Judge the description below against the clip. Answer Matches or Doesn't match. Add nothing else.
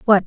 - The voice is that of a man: Doesn't match